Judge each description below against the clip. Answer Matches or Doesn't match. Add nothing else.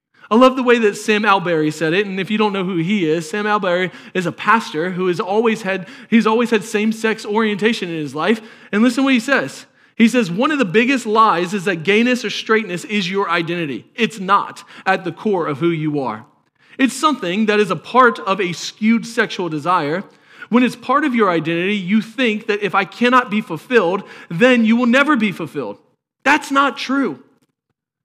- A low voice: Doesn't match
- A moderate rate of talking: Doesn't match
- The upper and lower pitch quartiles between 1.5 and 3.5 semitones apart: Doesn't match